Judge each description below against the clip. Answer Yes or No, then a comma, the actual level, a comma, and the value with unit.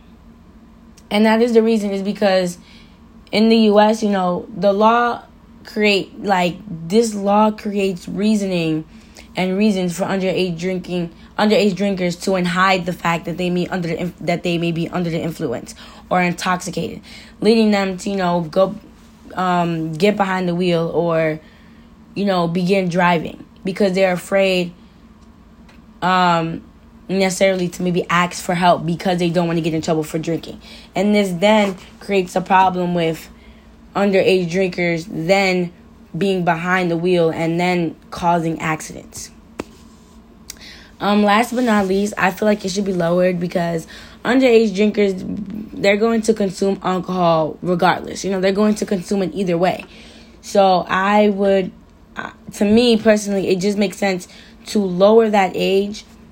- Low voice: No, high, 190 Hz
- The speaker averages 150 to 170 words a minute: Yes, average, 155 wpm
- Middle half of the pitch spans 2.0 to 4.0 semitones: Yes, average, 2.8 semitones